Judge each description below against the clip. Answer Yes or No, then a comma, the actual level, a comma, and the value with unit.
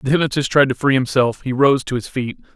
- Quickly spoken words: Yes, fast, 260 wpm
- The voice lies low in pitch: Yes, low, 130 Hz